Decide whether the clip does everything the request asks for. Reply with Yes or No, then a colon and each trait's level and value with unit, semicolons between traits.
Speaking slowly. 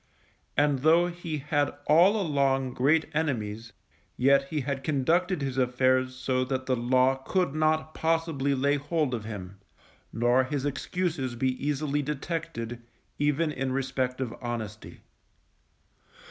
Yes: slow, 130 wpm